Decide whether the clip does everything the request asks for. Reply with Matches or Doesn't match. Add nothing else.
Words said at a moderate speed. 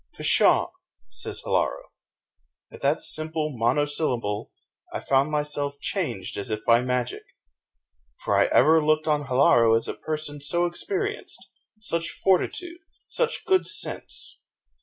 Doesn't match